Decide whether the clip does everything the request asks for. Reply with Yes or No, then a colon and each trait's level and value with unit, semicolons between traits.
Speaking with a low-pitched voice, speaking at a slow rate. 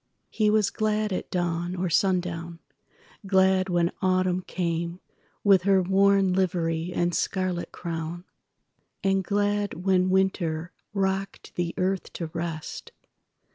No: medium, 185 Hz; slow, 105 wpm